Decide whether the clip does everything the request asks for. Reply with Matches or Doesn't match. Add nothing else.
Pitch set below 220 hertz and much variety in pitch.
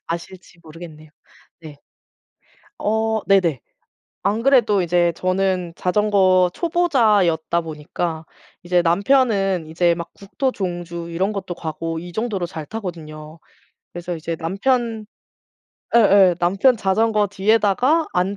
Doesn't match